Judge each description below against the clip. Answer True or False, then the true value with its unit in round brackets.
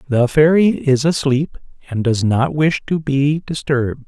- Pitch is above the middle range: False (140 Hz)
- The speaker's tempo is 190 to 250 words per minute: False (160 wpm)